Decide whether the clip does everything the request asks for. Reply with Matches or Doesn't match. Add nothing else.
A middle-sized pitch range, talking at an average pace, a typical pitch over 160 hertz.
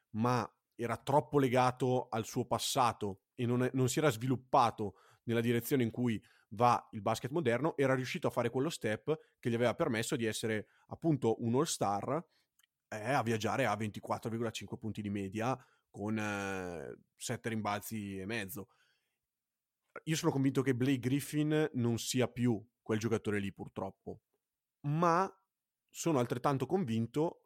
Doesn't match